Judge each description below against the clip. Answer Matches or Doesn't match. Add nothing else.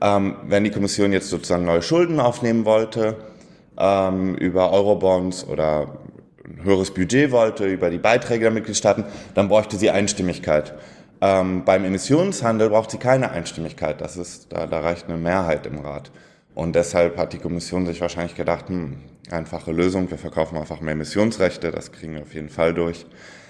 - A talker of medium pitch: Doesn't match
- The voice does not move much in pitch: Doesn't match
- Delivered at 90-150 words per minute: Doesn't match